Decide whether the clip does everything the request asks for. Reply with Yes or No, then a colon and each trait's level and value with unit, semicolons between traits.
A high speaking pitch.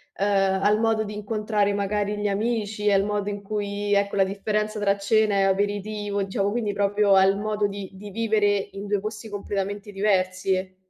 Yes: high, 205 Hz